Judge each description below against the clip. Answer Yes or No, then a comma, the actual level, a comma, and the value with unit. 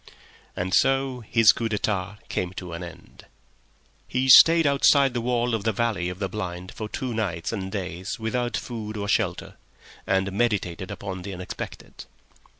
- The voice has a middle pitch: No, low, 105 Hz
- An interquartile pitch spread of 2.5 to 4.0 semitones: No, average, 4.4 semitones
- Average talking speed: Yes, average, 160 wpm